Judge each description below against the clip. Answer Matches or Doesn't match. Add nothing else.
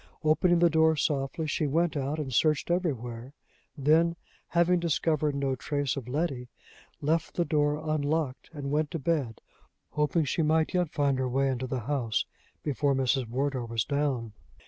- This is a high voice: Doesn't match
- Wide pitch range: Doesn't match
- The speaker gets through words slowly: Doesn't match